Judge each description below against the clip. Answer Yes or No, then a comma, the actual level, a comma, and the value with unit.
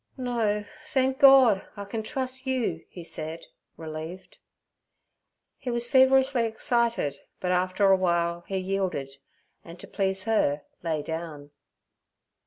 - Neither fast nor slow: No, slow, 125 wpm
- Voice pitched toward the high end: Yes, high, 195 Hz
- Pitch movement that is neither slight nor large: No, wide, 6.2 semitones